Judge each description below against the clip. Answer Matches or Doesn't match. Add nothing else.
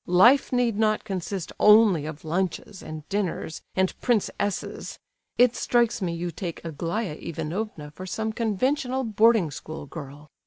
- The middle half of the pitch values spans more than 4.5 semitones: Matches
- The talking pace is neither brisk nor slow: Matches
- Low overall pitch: Doesn't match